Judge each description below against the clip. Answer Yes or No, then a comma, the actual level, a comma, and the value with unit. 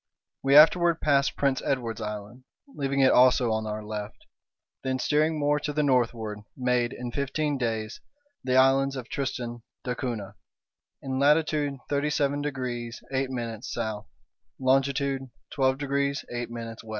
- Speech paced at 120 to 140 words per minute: Yes, slow, 135 wpm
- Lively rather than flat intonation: No, average, 2.8 semitones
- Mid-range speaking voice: No, low, 130 Hz